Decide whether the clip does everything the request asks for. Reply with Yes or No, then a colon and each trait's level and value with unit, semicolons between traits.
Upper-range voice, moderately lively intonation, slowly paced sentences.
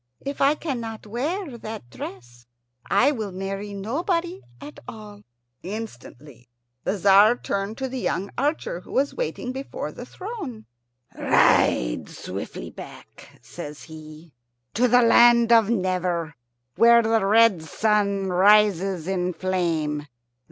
Yes: high, 210 Hz; average, 5.0 semitones; slow, 125 wpm